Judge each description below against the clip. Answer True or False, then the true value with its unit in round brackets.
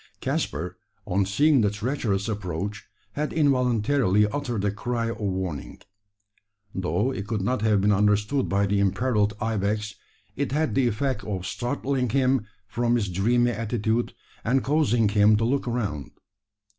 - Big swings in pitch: False (3.8 semitones)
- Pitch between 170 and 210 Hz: False (110 Hz)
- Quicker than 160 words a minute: False (145 wpm)